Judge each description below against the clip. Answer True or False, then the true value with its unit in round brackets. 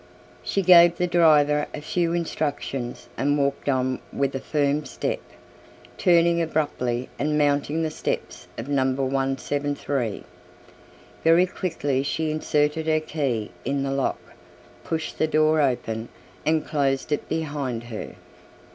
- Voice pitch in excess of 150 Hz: False (145 Hz)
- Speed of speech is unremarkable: False (130 wpm)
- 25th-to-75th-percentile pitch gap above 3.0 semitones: False (2.7 semitones)